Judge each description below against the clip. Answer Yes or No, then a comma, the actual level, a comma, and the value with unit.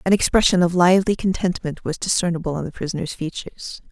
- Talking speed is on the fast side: No, average, 170 wpm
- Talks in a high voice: No, medium, 170 Hz